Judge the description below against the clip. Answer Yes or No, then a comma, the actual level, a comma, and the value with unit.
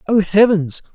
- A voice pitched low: No, high, 195 Hz